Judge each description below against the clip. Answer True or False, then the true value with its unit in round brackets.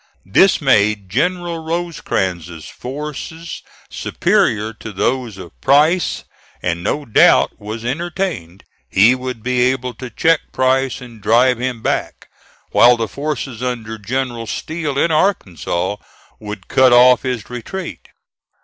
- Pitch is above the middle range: False (125 Hz)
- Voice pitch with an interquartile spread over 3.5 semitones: True (5.4 semitones)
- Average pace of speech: False (125 wpm)